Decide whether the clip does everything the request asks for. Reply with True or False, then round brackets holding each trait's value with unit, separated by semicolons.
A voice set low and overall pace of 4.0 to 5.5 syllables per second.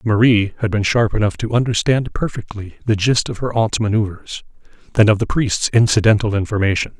False (110 Hz; 5.8 syllables/s)